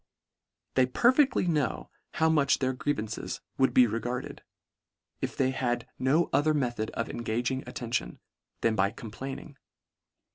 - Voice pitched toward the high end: No, low, 130 Hz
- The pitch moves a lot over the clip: No, average, 3.8 semitones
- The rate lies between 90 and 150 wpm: Yes, average, 140 wpm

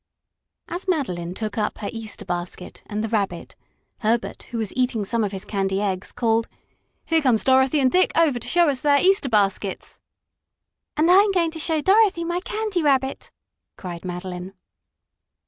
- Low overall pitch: No, high, 235 Hz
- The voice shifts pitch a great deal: Yes, wide, 8.5 semitones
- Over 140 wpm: Yes, average, 165 wpm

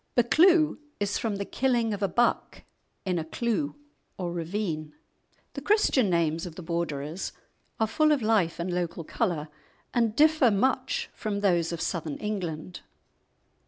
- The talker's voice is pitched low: No, high, 200 Hz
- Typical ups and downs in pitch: No, wide, 6.0 semitones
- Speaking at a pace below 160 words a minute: Yes, average, 150 wpm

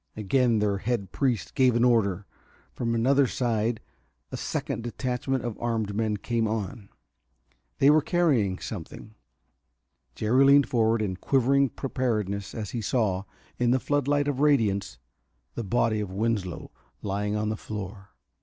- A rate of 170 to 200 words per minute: No, average, 145 wpm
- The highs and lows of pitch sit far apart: No, average, 3.7 semitones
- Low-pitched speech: Yes, low, 115 Hz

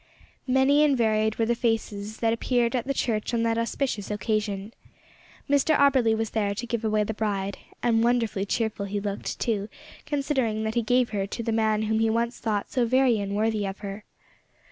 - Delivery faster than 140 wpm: Yes, average, 190 wpm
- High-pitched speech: Yes, high, 225 Hz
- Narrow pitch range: Yes, narrow, 2.3 semitones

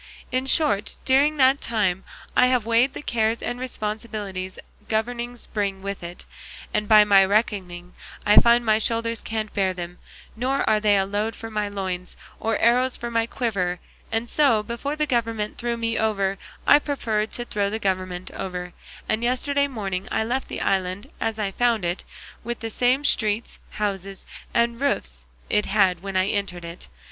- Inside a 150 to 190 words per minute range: Yes, average, 175 wpm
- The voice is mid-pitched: No, high, 215 Hz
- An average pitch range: Yes, average, 3.4 semitones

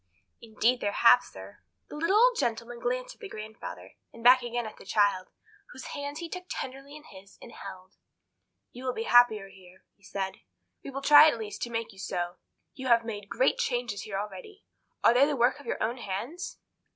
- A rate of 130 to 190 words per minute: No, average, 200 wpm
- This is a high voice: Yes, high, 235 Hz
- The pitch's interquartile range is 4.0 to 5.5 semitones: Yes, average, 5.2 semitones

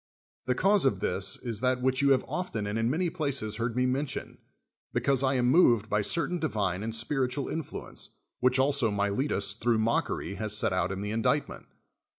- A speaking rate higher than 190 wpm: Yes, average, 200 wpm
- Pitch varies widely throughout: No, average, 4.5 semitones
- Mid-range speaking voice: No, low, 125 Hz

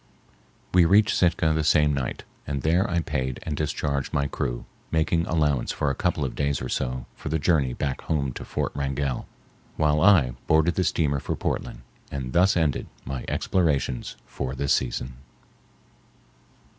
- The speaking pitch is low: Yes, very low, 75 Hz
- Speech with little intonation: No, average, 3.3 semitones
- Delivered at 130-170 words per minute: Yes, average, 165 wpm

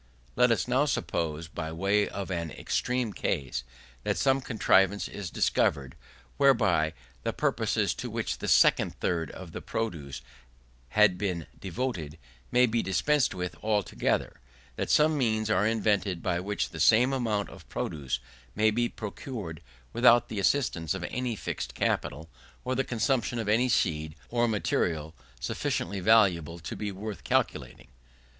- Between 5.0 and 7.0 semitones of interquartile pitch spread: Yes, wide, 5.6 semitones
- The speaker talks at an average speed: Yes, average, 150 wpm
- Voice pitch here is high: No, low, 100 Hz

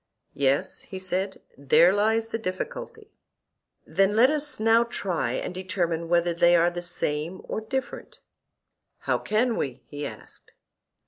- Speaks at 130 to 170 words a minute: Yes, average, 140 wpm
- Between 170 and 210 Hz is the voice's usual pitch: Yes, medium, 185 Hz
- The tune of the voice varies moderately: Yes, average, 4.8 semitones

